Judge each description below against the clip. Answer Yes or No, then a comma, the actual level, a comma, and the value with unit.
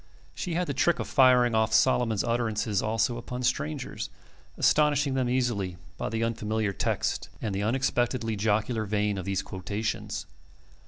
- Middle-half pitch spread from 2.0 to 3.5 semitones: Yes, average, 3.0 semitones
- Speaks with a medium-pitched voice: No, low, 115 Hz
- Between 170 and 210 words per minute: No, average, 150 wpm